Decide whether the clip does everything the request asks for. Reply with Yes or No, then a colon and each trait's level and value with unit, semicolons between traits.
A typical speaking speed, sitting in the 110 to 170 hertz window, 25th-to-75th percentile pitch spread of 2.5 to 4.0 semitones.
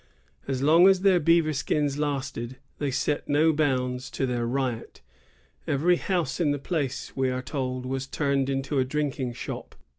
Yes: average, 170 wpm; medium, 140 Hz; average, 2.8 semitones